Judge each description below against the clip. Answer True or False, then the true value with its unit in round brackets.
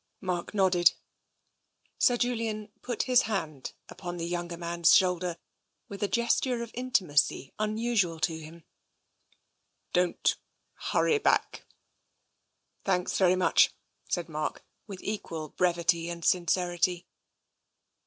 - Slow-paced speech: True (115 wpm)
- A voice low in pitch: False (180 Hz)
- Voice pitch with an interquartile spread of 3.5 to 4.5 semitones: True (3.8 semitones)